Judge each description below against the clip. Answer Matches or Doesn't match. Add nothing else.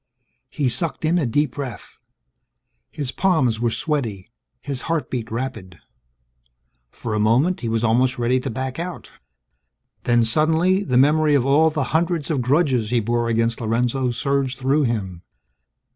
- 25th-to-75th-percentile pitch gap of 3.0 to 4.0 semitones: Doesn't match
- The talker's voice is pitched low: Matches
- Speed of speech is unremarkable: Matches